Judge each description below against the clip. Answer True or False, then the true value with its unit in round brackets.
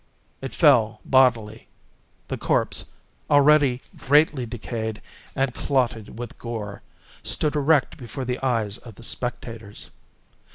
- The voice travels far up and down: False (3.3 semitones)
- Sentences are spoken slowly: True (115 wpm)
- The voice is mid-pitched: False (125 Hz)